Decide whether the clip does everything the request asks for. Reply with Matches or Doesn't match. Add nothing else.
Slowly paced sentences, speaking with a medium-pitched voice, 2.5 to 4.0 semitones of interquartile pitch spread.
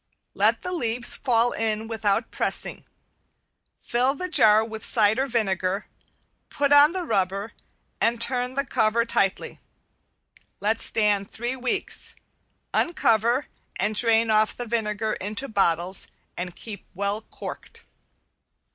Doesn't match